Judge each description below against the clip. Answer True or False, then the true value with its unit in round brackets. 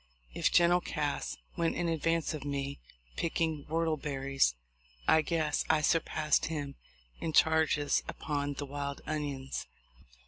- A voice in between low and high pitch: True (150 Hz)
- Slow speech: True (125 wpm)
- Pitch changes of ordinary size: False (2.3 semitones)